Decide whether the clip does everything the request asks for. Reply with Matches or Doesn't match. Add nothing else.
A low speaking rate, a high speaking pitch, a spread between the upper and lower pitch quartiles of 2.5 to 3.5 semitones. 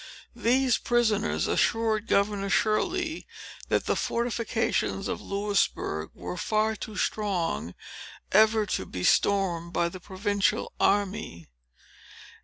Matches